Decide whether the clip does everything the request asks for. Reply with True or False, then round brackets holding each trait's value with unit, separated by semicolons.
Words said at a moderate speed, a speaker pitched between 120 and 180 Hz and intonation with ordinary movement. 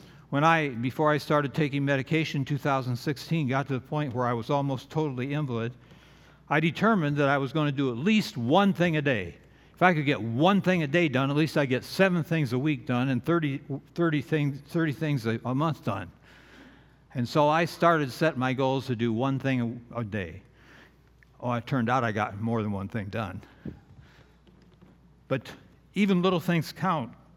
True (195 wpm; 140 Hz; 4.2 semitones)